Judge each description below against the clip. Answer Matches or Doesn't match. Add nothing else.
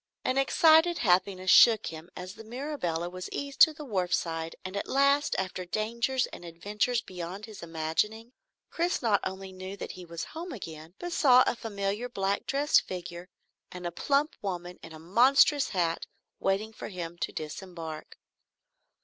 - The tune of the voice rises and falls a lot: Matches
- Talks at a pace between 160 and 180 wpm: Matches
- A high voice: Matches